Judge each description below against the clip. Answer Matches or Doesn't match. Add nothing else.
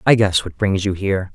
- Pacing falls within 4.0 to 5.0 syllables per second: Doesn't match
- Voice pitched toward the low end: Matches